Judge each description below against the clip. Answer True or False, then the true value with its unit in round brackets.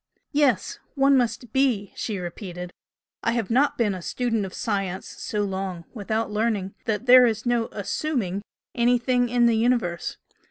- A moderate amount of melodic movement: True (3.9 semitones)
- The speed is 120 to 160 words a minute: True (155 wpm)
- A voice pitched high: True (225 Hz)